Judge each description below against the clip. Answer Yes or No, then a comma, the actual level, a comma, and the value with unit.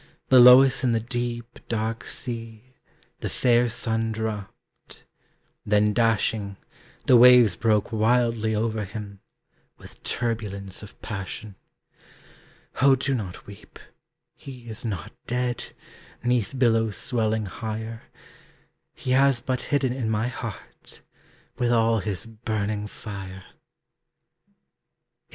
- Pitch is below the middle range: Yes, low, 115 Hz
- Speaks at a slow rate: Yes, slow, 115 wpm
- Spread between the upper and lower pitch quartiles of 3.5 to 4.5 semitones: No, narrow, 2.4 semitones